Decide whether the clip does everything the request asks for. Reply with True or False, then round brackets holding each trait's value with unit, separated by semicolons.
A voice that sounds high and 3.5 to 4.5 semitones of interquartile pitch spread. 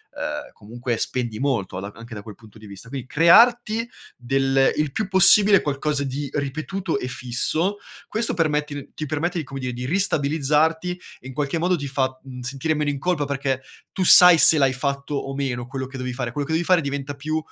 False (140 Hz; 3.8 semitones)